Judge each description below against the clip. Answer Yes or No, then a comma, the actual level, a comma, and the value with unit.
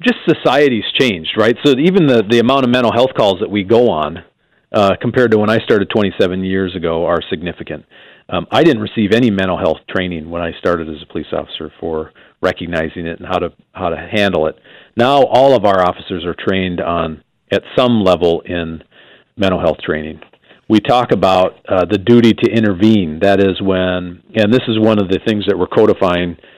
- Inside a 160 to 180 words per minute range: No, average, 200 wpm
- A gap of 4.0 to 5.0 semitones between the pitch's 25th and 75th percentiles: Yes, average, 4.3 semitones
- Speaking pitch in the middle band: No, very low, 95 Hz